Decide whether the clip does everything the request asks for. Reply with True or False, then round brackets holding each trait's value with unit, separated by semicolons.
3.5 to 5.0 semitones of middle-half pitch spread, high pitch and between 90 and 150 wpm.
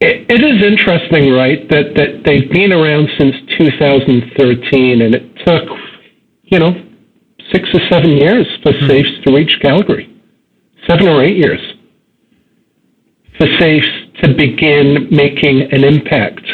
False (4.0 semitones; 150 Hz; 135 wpm)